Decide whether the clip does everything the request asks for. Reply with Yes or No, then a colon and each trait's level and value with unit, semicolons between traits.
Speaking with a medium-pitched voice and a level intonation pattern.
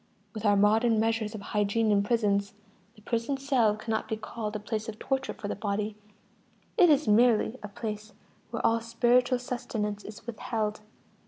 No: high, 220 Hz; narrow, 2.1 semitones